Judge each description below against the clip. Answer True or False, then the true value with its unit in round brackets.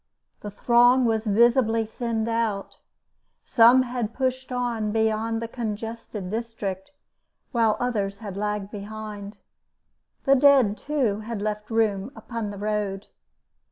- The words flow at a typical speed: False (120 wpm)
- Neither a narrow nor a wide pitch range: False (2.3 semitones)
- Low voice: False (225 Hz)